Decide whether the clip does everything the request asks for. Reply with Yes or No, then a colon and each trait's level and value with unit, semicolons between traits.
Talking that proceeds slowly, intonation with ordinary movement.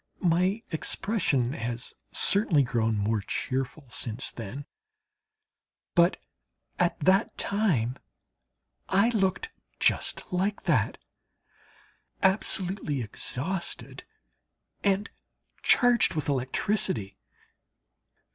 No: slow, 80 wpm; wide, 8.0 semitones